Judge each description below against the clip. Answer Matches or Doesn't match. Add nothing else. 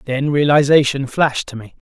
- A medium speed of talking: Matches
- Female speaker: Doesn't match